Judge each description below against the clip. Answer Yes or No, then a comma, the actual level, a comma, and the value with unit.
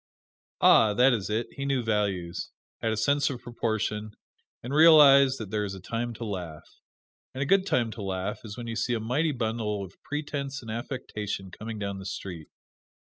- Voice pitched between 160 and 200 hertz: No, low, 115 Hz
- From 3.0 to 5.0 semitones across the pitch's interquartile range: Yes, average, 4.2 semitones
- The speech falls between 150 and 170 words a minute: No, average, 190 wpm